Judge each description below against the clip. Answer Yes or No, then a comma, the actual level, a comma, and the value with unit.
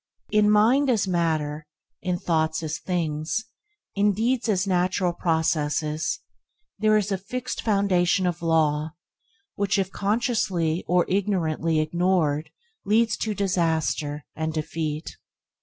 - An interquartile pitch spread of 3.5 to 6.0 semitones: Yes, average, 4.3 semitones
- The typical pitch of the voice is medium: Yes, medium, 180 Hz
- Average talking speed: No, slow, 130 wpm